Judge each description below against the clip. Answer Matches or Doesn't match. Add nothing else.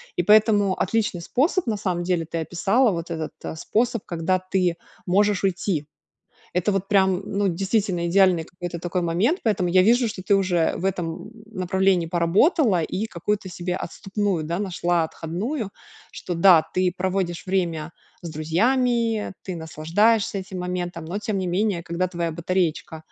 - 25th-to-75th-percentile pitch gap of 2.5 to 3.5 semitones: Matches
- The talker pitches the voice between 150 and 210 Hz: Matches